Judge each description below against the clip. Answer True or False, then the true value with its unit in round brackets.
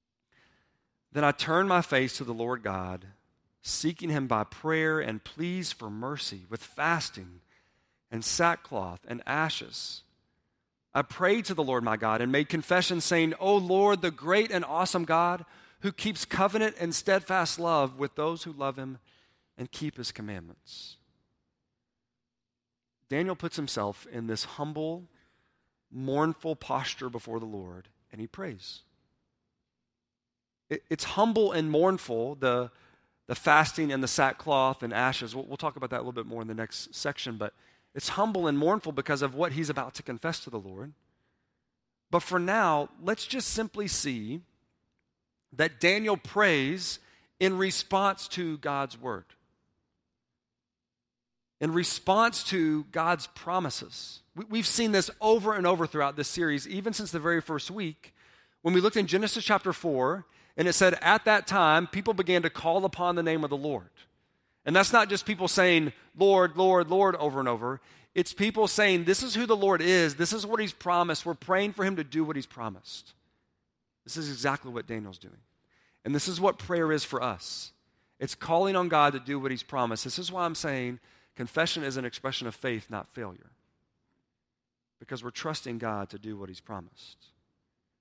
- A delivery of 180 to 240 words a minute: False (170 wpm)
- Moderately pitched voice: True (155 Hz)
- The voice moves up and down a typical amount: False (6.8 semitones)